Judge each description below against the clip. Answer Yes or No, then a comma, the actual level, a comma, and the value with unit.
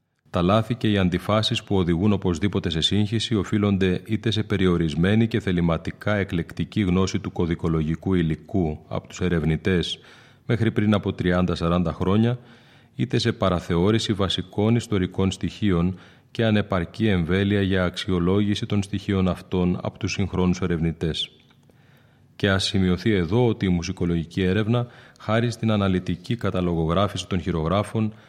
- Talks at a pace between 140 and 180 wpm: No, average, 130 wpm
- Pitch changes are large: No, average, 3.4 semitones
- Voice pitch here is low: Yes, very low, 95 Hz